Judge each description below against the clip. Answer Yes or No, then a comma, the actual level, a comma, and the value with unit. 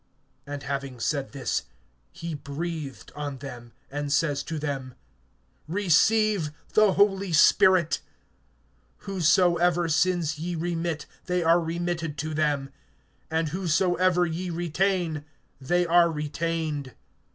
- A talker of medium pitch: Yes, medium, 165 Hz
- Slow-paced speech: Yes, slow, 110 wpm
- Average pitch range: Yes, average, 3.1 semitones